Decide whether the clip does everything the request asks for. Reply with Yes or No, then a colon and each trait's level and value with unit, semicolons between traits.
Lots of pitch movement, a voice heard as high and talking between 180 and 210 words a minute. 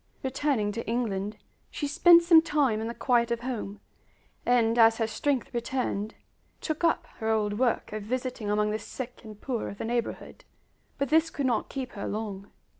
No: average, 3.7 semitones; high, 235 Hz; average, 185 wpm